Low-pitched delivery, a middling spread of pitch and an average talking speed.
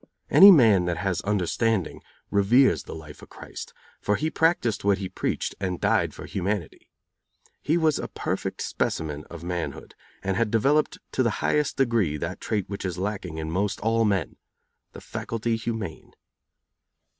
Yes: low, 100 Hz; average, 4.6 semitones; average, 160 wpm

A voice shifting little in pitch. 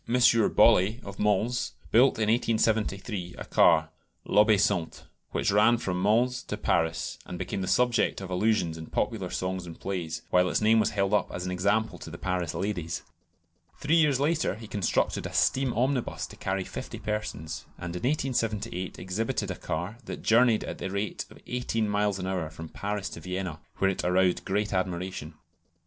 No: average, 3.6 semitones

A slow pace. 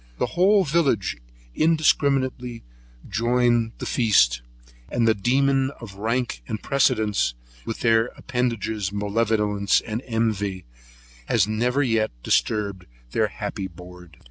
Yes: slow, 115 wpm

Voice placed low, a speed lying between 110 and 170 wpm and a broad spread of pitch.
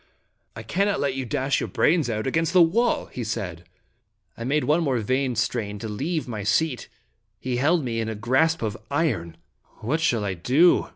No: low, 130 Hz; fast, 205 wpm; wide, 6.4 semitones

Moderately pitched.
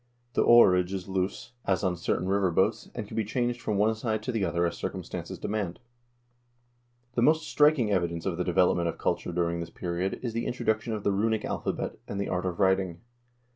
No: low, 100 Hz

